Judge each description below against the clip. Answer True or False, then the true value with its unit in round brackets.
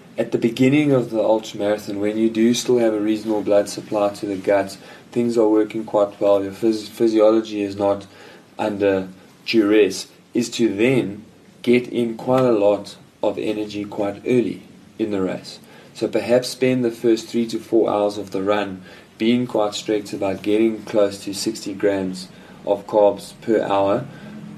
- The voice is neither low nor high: False (105 Hz)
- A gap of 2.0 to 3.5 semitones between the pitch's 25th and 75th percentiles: True (2.4 semitones)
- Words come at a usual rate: True (170 wpm)